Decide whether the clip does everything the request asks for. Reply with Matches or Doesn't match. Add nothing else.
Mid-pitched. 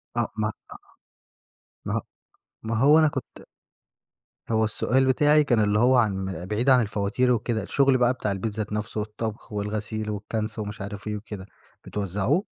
Doesn't match